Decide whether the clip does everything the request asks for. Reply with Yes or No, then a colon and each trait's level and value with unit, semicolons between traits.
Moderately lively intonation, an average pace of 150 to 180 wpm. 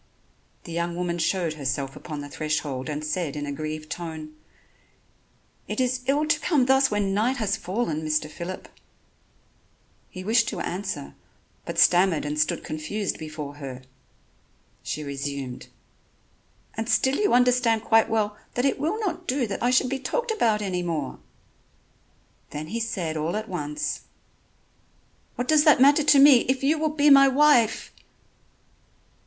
No: wide, 8.8 semitones; average, 155 wpm